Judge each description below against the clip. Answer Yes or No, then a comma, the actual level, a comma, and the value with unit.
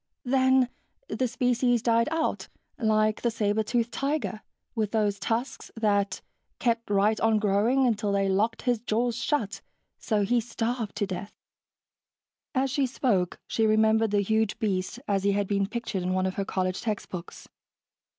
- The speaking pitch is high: Yes, high, 220 Hz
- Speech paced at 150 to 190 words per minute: Yes, average, 160 wpm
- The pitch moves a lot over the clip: No, average, 3.0 semitones